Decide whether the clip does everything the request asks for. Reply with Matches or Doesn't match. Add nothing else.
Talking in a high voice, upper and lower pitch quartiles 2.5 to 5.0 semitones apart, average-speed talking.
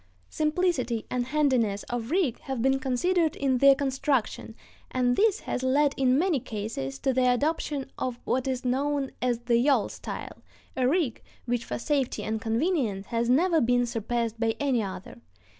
Matches